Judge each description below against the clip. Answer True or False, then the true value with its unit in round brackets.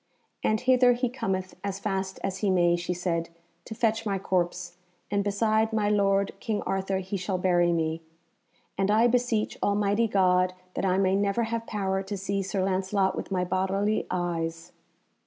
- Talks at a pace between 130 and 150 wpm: False (175 wpm)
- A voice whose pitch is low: False (195 Hz)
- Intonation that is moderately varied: False (2.3 semitones)